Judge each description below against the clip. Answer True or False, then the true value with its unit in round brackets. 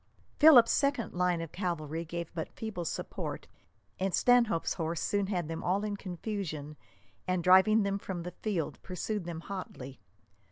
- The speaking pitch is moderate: True (180 Hz)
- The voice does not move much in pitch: False (3.7 semitones)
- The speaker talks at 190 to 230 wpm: False (155 wpm)